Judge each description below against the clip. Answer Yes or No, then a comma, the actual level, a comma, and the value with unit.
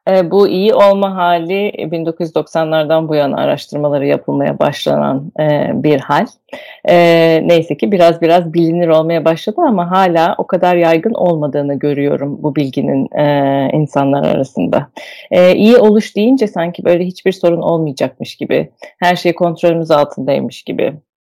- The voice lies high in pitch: No, medium, 170 Hz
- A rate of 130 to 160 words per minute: Yes, fast, 140 wpm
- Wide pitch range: No, average, 3.2 semitones